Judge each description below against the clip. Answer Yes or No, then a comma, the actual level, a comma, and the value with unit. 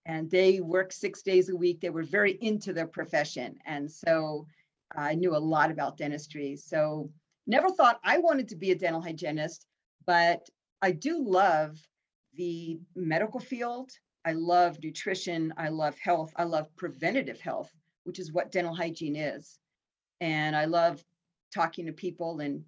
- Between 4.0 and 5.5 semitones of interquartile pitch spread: No, average, 2.9 semitones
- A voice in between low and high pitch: Yes, medium, 170 Hz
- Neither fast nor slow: Yes, average, 160 wpm